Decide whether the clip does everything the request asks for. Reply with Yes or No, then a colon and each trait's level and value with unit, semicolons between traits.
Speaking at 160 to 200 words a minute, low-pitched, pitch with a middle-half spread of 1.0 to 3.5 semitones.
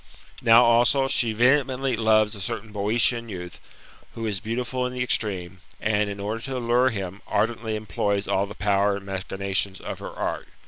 Yes: average, 180 wpm; low, 110 Hz; average, 3.1 semitones